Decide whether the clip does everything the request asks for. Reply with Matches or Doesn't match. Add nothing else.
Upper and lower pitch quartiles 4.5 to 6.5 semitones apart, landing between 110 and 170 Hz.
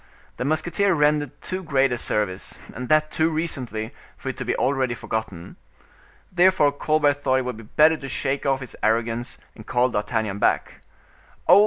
Matches